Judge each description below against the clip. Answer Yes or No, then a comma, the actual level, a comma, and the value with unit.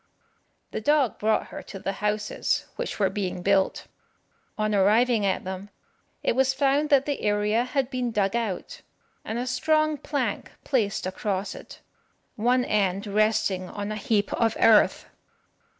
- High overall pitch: Yes, high, 215 Hz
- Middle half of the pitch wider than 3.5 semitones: Yes, average, 3.9 semitones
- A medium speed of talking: Yes, average, 150 wpm